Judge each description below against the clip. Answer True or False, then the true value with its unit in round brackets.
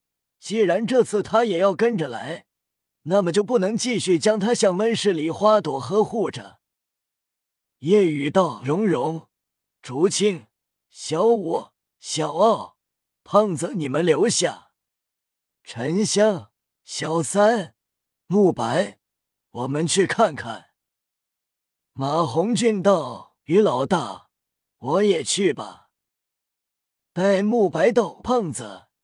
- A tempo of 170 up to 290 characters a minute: False (150 characters per minute)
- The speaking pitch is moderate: True (175 Hz)